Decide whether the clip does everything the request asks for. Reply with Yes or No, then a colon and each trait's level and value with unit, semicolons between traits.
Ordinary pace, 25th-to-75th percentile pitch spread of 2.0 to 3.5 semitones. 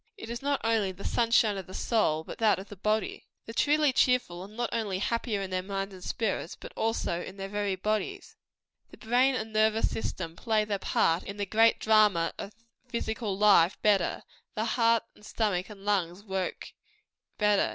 Yes: average, 190 wpm; average, 2.9 semitones